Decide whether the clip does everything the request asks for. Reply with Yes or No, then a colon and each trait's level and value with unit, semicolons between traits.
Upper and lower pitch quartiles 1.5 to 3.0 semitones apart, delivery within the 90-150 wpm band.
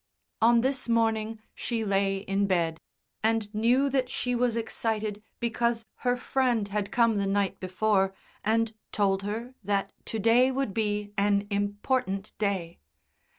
Yes: average, 2.7 semitones; average, 145 wpm